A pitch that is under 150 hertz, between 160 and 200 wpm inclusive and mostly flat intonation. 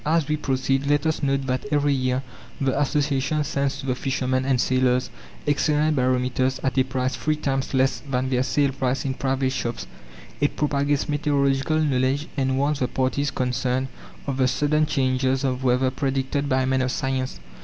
Yes: low, 135 Hz; average, 175 wpm; narrow, 1.7 semitones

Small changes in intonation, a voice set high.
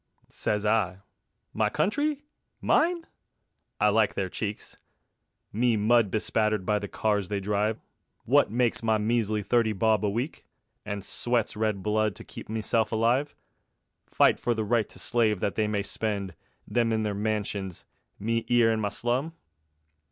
No: narrow, 2.0 semitones; low, 110 Hz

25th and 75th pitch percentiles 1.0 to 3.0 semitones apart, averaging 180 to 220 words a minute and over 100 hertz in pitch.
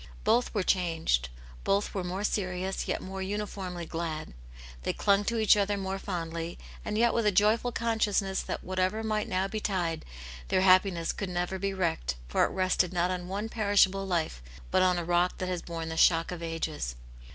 Yes: average, 2.7 semitones; average, 185 wpm; medium, 185 Hz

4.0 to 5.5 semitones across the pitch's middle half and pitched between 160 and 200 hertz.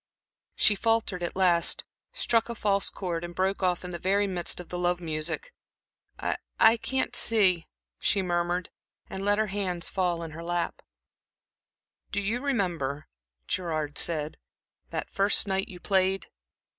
No: average, 2.7 semitones; medium, 185 Hz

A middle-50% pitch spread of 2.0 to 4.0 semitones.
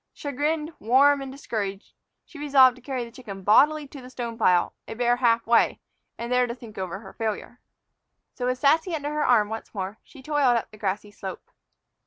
No: average, 4.4 semitones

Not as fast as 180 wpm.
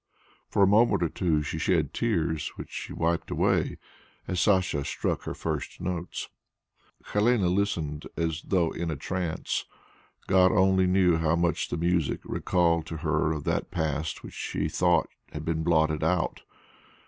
Yes: average, 160 wpm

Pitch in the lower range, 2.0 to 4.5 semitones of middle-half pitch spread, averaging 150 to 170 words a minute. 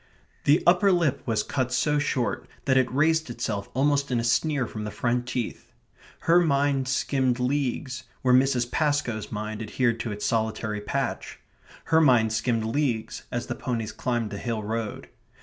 Yes: low, 125 Hz; average, 4.0 semitones; average, 165 wpm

